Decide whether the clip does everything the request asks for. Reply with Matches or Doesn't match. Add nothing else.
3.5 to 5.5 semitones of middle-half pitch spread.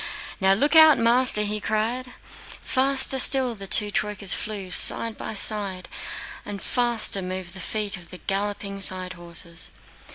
Matches